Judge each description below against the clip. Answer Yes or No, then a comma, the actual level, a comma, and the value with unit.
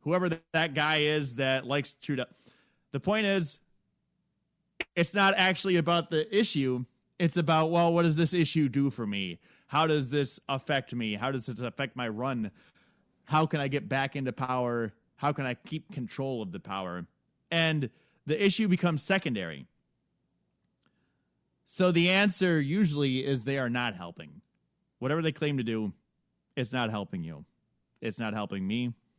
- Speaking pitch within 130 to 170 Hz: Yes, medium, 140 Hz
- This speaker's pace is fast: No, average, 160 wpm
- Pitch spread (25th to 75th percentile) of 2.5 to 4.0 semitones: No, average, 5.1 semitones